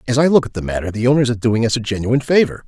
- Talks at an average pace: No, fast, 315 wpm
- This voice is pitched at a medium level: No, low, 120 Hz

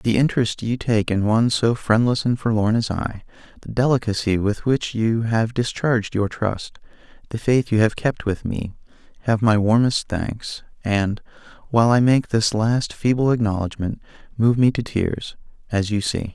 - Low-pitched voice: Yes, low, 110 Hz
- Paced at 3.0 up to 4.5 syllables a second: No, 4.7 syllables/s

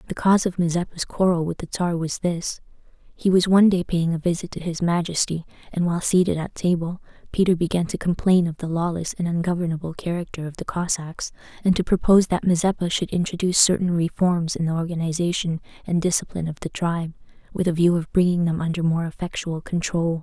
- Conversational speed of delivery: Yes, average, 195 wpm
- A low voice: No, medium, 170 Hz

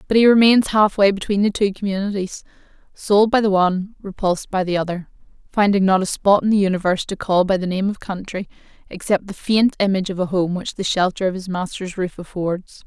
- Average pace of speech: No, fast, 215 wpm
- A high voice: Yes, high, 195 Hz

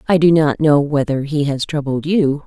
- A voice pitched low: No, medium, 150 Hz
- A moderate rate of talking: No, fast, 220 wpm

